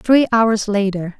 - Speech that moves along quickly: No, average, 150 wpm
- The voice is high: Yes, high, 215 Hz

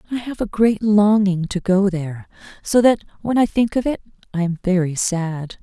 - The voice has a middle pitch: No, high, 200 Hz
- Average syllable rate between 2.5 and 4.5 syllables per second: No, 5.0 syllables/s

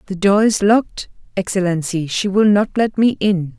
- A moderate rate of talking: Yes, average, 185 wpm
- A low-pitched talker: No, high, 195 Hz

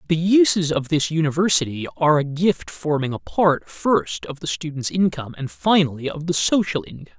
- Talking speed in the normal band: Yes, average, 185 wpm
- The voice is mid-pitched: Yes, medium, 155 Hz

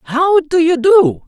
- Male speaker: No, female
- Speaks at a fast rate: No, average, 190 wpm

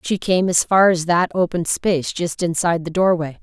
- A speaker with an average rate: No, fast, 210 wpm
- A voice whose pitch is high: No, medium, 175 Hz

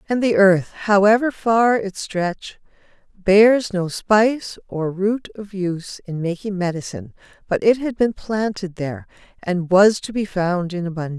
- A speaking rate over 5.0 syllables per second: No, 4.6 syllables/s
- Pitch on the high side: Yes, high, 195 Hz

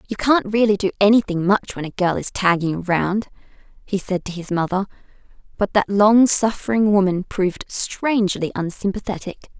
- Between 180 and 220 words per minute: No, average, 155 wpm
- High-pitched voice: Yes, high, 195 Hz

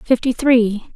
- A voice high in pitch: Yes, high, 235 Hz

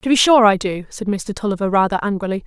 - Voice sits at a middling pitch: No, high, 205 Hz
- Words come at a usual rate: No, fast, 245 wpm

